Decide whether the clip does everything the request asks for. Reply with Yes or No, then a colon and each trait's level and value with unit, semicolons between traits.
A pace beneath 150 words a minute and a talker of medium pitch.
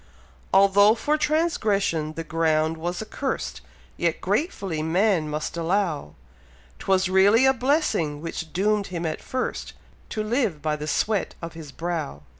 Yes: average, 140 wpm; medium, 180 Hz